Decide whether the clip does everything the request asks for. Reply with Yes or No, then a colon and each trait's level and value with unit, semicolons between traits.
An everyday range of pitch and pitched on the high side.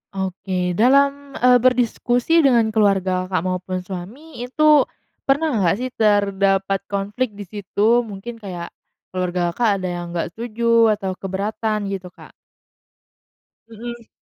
Yes: average, 4.3 semitones; high, 210 Hz